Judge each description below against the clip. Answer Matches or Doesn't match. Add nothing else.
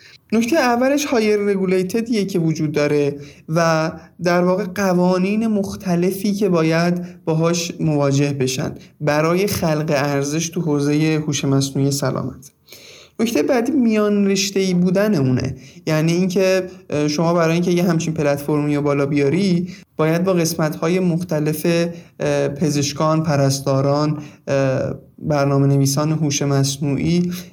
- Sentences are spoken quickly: Doesn't match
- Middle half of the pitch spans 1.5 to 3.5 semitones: Doesn't match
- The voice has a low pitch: Doesn't match